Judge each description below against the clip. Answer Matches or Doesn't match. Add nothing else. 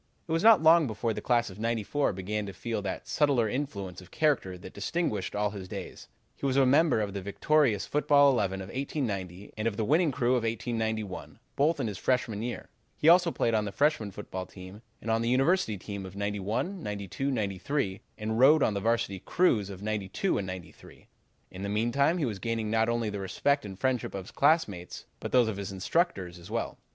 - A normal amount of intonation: Doesn't match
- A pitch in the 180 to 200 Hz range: Doesn't match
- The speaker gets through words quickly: Matches